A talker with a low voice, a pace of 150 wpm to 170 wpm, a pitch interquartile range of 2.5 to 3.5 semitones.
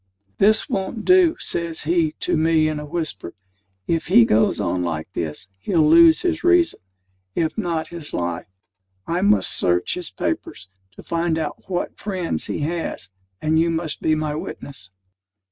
No: medium, 160 Hz; average, 160 wpm; average, 3.1 semitones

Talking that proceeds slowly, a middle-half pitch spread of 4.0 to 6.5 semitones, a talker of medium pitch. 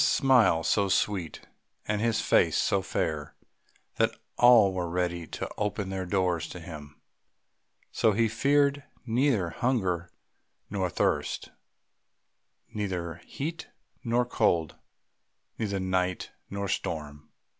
No: slow, 120 wpm; average, 4.8 semitones; very low, 95 Hz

